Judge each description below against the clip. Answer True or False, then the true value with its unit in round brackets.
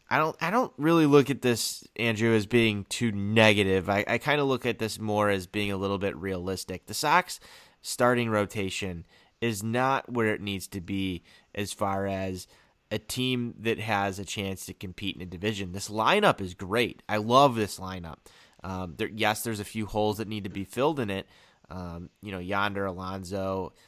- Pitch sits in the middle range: False (105 Hz)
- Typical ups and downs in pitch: True (3.0 semitones)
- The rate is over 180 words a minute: True (200 wpm)